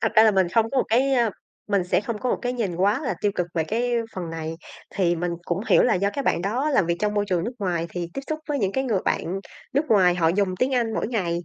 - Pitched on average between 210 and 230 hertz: No, high, 200 Hz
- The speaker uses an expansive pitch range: No, average, 4.8 semitones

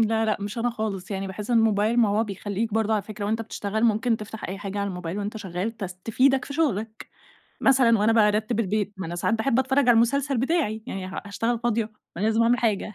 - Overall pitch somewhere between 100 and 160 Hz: No, high, 220 Hz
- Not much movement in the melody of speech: Yes, narrow, 2.3 semitones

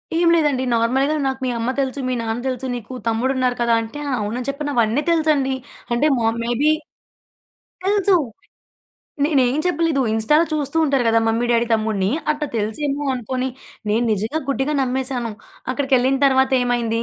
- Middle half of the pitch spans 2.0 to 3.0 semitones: No, average, 3.7 semitones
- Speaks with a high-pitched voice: Yes, very high, 260 Hz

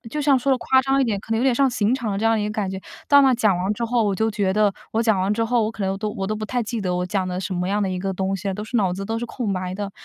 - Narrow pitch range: No, average, 3.3 semitones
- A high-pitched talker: Yes, high, 210 Hz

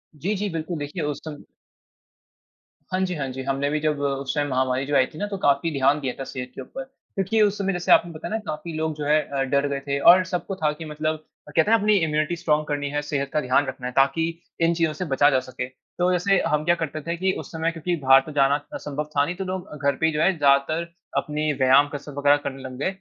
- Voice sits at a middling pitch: Yes, medium, 150 Hz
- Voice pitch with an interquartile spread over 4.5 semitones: No, average, 3.6 semitones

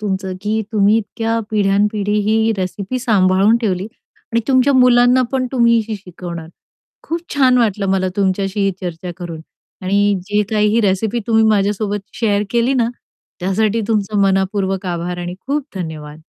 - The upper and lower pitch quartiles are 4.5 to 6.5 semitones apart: No, average, 3.1 semitones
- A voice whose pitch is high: Yes, high, 205 Hz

